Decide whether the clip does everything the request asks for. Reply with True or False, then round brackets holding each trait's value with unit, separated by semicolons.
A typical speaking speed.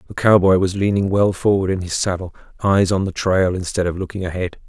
False (220 wpm)